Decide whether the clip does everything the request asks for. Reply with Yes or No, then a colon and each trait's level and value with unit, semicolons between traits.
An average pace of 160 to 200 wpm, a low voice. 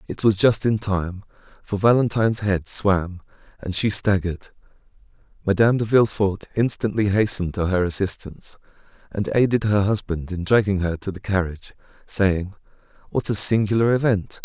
No: average, 140 wpm; low, 100 Hz